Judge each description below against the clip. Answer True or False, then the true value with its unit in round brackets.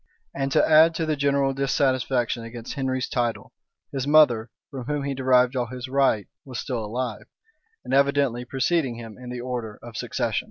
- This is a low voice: True (130 Hz)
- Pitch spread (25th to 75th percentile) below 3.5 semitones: True (2.4 semitones)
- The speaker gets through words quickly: False (175 wpm)